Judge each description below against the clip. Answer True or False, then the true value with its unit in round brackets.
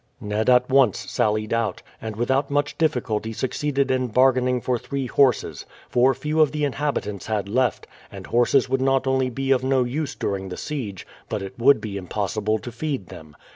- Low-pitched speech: True (125 Hz)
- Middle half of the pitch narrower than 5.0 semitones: True (4.0 semitones)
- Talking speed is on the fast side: False (185 wpm)